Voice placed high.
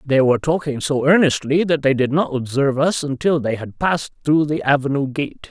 No: medium, 140 Hz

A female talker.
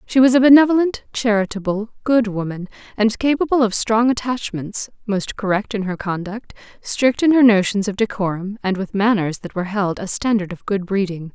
Yes: female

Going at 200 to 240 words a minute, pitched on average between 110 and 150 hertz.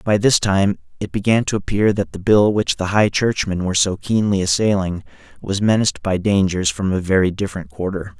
No: fast, 205 wpm; low, 100 Hz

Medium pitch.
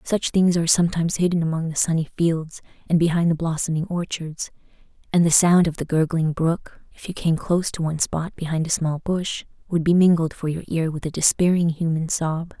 Yes: medium, 165 Hz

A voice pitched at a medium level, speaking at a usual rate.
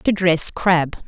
Yes: medium, 175 Hz; average, 165 wpm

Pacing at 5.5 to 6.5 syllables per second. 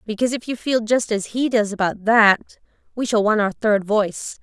No: 5.1 syllables/s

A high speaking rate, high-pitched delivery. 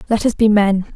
Yes: fast, 250 wpm; high, 210 Hz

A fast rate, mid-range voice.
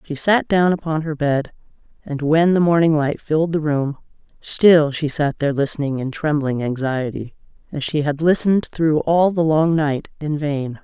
No: average, 185 wpm; medium, 155 Hz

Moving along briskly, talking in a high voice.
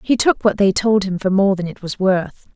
Yes: fast, 280 wpm; high, 195 Hz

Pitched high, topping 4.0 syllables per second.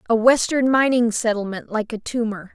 Yes: high, 230 Hz; 5.1 syllables/s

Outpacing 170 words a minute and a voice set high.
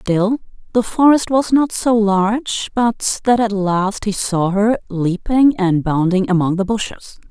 No: average, 165 wpm; high, 210 Hz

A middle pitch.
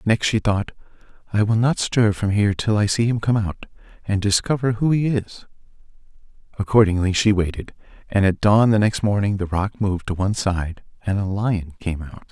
No: low, 105 Hz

